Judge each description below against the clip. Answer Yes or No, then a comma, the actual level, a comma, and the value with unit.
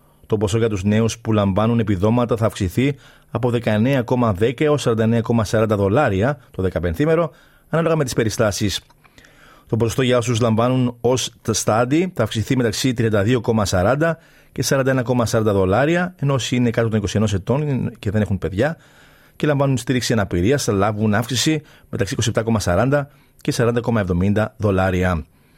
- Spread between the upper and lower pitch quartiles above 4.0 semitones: No, average, 3.7 semitones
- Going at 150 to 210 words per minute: No, average, 140 wpm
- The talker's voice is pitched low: Yes, low, 115 Hz